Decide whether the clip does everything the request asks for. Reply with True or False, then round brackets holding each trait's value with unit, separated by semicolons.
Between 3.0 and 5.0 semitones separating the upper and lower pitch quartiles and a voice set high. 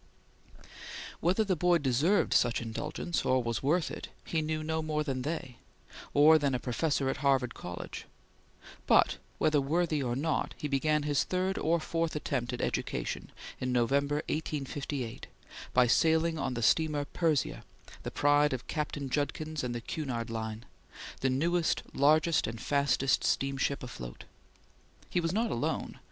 False (3.6 semitones; 145 Hz)